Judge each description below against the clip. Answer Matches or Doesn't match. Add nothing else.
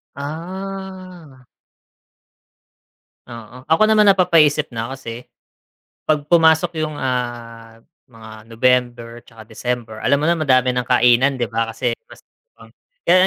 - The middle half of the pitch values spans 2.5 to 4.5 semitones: Doesn't match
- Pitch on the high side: Doesn't match